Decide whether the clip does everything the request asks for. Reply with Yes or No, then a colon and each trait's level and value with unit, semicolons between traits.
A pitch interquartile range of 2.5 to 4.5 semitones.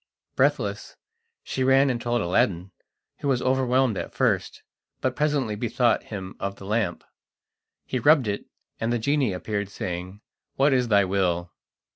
No: average, 4.9 semitones